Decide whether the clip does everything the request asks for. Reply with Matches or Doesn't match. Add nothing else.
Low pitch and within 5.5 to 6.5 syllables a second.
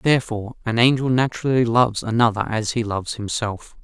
Matches